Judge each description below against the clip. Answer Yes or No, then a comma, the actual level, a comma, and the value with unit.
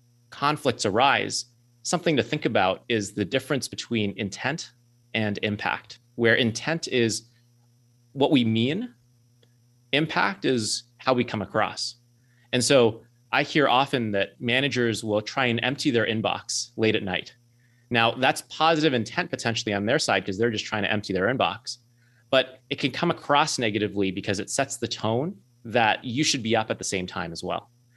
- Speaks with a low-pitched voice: Yes, low, 120 Hz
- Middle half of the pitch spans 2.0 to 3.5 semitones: Yes, average, 2.8 semitones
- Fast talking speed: No, average, 170 wpm